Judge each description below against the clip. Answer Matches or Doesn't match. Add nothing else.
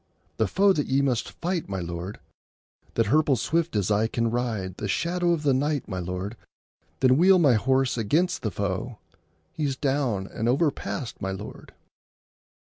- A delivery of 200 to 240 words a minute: Doesn't match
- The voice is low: Matches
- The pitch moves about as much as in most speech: Doesn't match